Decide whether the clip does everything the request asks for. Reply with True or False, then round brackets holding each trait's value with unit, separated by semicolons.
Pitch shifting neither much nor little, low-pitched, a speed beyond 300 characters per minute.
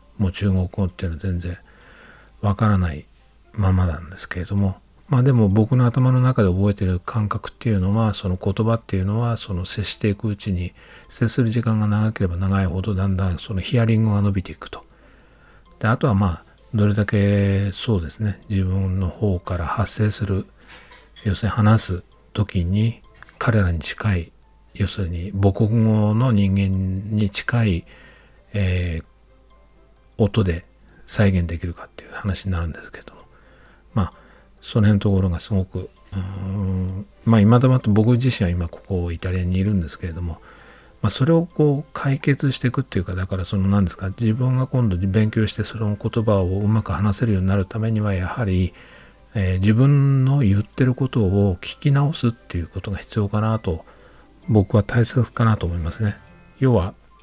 True (3.0 semitones; 100 Hz; 340 characters per minute)